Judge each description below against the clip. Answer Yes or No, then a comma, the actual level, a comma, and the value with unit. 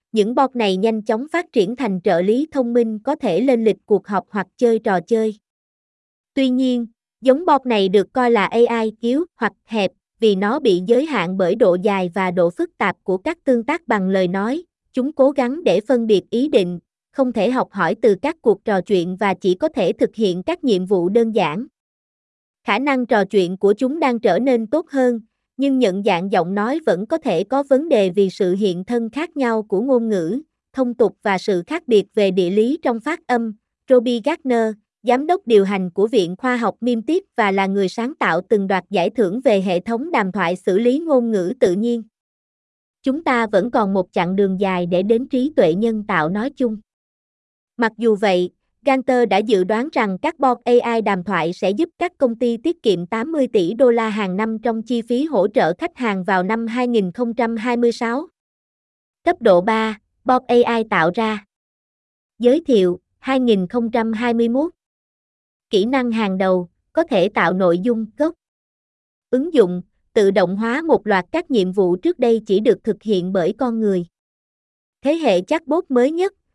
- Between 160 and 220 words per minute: Yes, average, 200 wpm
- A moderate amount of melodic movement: Yes, average, 4.6 semitones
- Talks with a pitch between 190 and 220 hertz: No, high, 230 Hz